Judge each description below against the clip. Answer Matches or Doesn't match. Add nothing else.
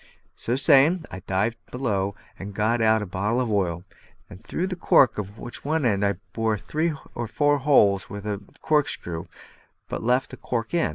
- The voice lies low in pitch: Matches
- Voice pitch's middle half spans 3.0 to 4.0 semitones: Doesn't match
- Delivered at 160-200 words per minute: Matches